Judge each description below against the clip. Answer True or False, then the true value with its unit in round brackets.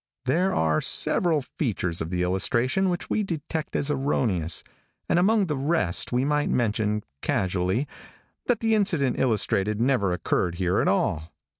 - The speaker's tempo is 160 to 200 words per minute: False (150 wpm)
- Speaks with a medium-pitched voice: False (125 Hz)